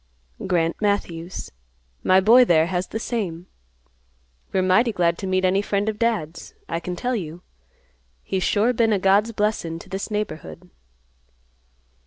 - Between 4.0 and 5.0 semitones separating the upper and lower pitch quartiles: No, average, 3.6 semitones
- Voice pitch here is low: No, high, 190 Hz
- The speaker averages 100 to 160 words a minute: Yes, average, 150 wpm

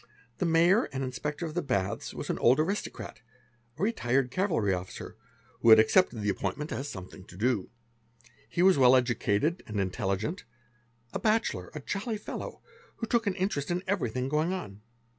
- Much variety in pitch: Yes, wide, 8.9 semitones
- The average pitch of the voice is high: No, medium, 140 Hz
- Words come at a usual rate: Yes, average, 175 wpm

